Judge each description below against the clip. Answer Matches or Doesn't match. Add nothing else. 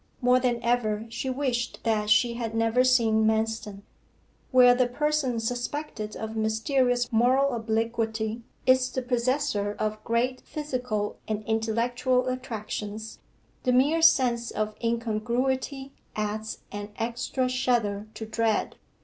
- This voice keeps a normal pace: Doesn't match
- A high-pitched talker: Matches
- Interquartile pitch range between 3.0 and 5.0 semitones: Doesn't match